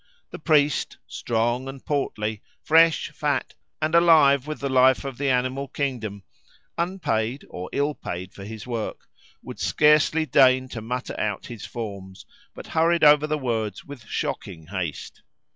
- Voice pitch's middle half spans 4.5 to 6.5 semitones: Yes, average, 5.2 semitones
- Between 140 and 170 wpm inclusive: Yes, average, 150 wpm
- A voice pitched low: Yes, low, 130 Hz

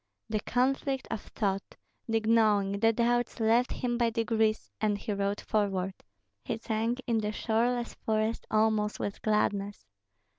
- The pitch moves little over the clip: Yes, narrow, 1.9 semitones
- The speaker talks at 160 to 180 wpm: No, average, 145 wpm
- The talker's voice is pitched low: No, high, 220 Hz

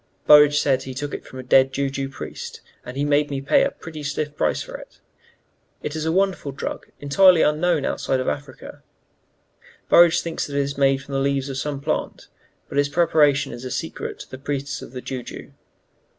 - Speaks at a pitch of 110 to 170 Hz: Yes, medium, 140 Hz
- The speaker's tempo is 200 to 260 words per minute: Yes, fast, 205 wpm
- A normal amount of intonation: No, narrow, 1.8 semitones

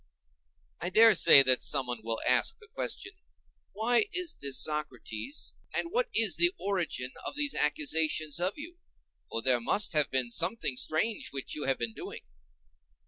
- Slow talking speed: No, average, 160 wpm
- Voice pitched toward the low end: No, medium, 155 Hz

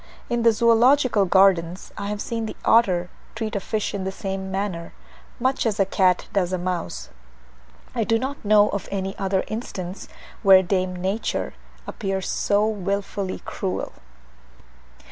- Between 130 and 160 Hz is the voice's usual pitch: No, high, 200 Hz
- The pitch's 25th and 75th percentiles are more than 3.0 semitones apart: No, average, 2.7 semitones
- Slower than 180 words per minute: Yes, average, 150 wpm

